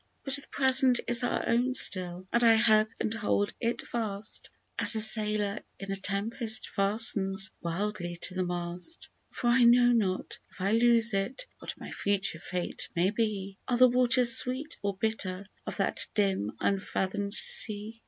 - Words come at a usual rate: Yes, average, 165 wpm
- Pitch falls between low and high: No, high, 215 Hz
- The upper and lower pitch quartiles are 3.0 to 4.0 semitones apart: Yes, average, 3.4 semitones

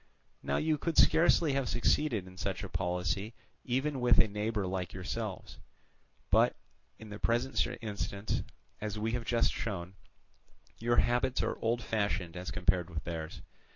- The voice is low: Yes, low, 105 Hz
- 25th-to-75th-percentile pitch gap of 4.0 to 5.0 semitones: Yes, average, 4.6 semitones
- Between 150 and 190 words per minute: Yes, average, 155 wpm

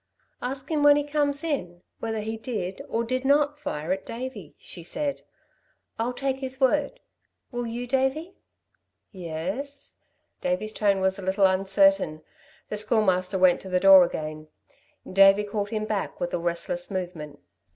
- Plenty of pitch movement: Yes, wide, 6.3 semitones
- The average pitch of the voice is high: Yes, high, 215 Hz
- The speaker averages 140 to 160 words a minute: Yes, average, 155 wpm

